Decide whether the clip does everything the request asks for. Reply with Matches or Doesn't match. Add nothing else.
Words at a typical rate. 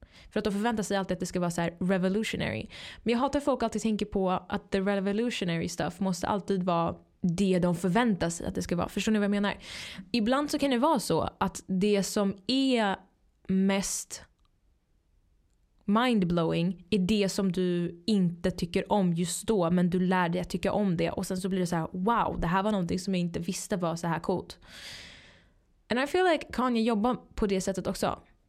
Doesn't match